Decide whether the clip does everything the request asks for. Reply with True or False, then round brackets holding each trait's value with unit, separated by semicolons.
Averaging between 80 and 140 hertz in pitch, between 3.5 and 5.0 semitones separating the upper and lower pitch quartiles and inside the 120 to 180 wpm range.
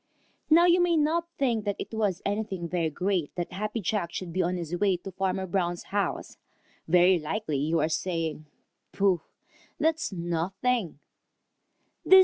False (190 Hz; 3.9 semitones; 150 wpm)